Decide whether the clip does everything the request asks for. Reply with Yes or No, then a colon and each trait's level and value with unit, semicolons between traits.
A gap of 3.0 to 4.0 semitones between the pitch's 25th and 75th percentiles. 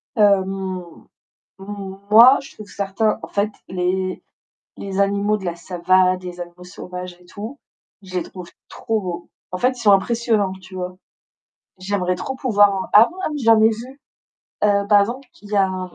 No: narrow, 2.5 semitones